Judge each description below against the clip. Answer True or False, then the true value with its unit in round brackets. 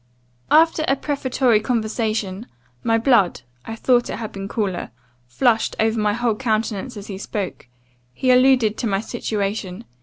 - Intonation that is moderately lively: True (3.2 semitones)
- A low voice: False (225 Hz)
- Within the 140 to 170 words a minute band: True (150 wpm)